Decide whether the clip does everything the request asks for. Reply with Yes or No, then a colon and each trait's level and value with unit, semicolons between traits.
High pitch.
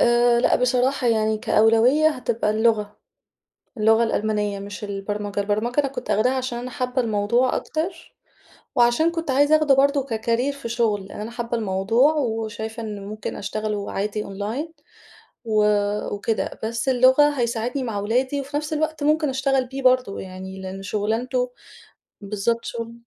Yes: high, 235 Hz